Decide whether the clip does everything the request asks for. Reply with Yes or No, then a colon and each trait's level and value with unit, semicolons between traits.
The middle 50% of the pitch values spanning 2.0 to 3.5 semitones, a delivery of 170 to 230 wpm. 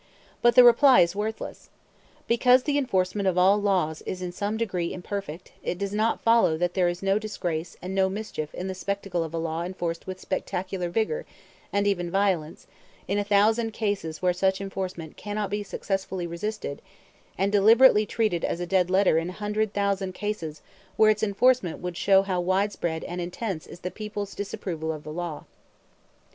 Yes: average, 3.0 semitones; average, 180 wpm